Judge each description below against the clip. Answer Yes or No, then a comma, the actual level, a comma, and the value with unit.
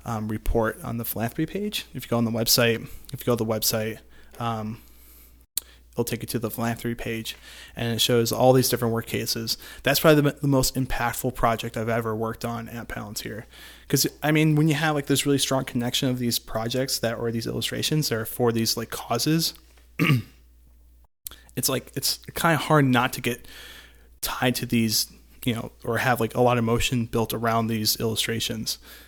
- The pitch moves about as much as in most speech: No, narrow, 2.3 semitones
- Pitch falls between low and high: No, low, 115 Hz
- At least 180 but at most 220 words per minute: Yes, average, 200 wpm